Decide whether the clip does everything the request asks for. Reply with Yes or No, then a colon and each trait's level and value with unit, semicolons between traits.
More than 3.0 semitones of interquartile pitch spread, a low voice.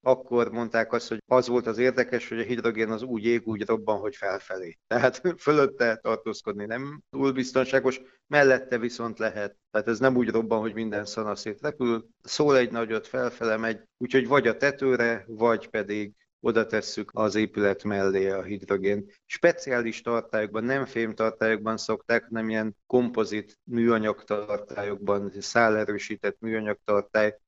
No: average, 2.7 semitones; low, 115 Hz